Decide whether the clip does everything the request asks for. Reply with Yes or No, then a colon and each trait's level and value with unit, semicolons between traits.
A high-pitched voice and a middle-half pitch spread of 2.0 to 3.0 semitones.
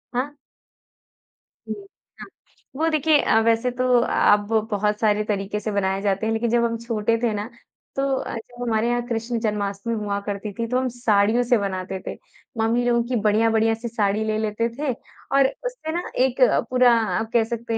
Yes: high, 225 Hz; narrow, 2.6 semitones